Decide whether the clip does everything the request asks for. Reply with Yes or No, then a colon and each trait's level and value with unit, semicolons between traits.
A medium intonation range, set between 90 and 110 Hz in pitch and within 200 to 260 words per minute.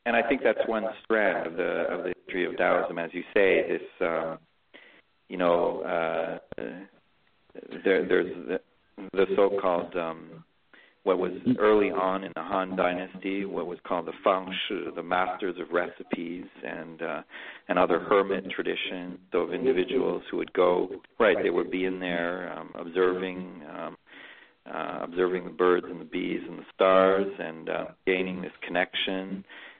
No: average, 3.8 semitones; very low, 95 Hz; average, 160 wpm